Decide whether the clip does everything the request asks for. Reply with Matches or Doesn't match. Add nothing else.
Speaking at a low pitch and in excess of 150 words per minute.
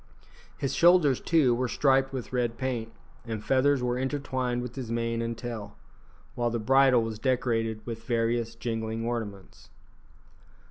Doesn't match